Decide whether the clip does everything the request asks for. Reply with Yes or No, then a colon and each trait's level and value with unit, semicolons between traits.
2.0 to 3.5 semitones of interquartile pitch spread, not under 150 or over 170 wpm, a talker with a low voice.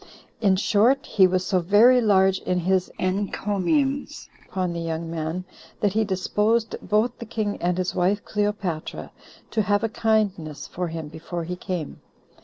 No: average, 3.0 semitones; average, 160 wpm; high, 190 Hz